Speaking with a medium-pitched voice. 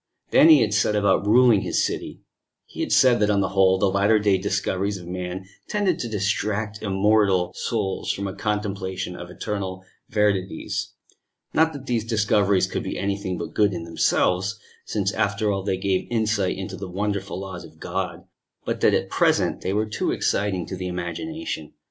No: low, 100 Hz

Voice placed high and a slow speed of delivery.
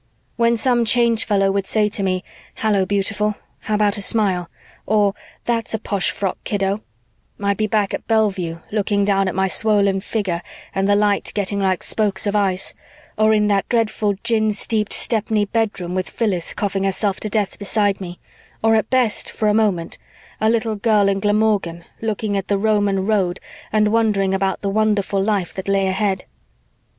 No: high, 205 Hz; average, 180 wpm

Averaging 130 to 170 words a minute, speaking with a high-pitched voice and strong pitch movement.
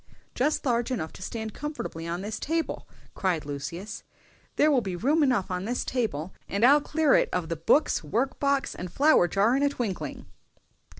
No: average, 190 wpm; high, 220 Hz; wide, 7.7 semitones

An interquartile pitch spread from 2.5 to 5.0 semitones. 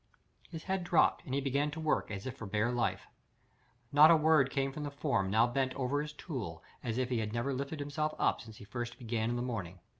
Yes: average, 4.1 semitones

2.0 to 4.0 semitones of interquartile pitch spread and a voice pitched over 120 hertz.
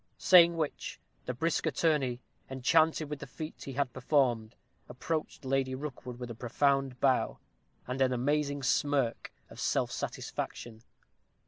Yes: average, 3.1 semitones; low, 135 Hz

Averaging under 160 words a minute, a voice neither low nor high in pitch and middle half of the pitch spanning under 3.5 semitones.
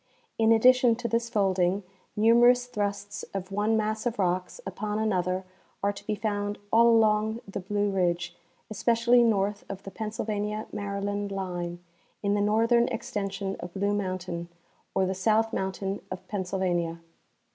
No: average, 150 wpm; high, 205 Hz; narrow, 2.6 semitones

